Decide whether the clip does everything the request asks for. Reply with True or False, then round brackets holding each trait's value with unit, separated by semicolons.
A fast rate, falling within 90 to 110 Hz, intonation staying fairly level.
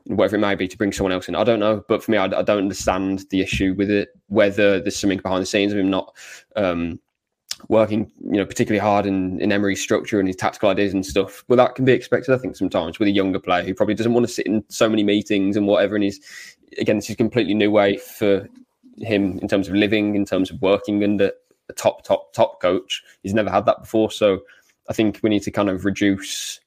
True (250 wpm; 100 Hz; 2.0 semitones)